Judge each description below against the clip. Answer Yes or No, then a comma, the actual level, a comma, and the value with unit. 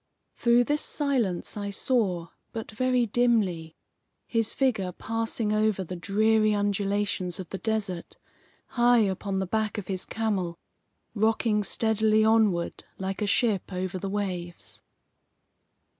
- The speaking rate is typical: No, slow, 130 wpm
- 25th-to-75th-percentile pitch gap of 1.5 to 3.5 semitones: Yes, average, 2.9 semitones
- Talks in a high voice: Yes, high, 210 Hz